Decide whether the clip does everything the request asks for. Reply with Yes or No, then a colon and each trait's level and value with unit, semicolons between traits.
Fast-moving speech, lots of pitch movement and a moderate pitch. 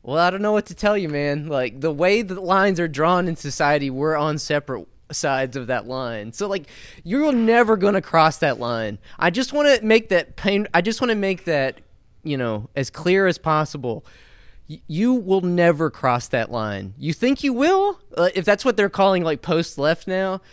Yes: fast, 215 wpm; wide, 6.3 semitones; medium, 165 Hz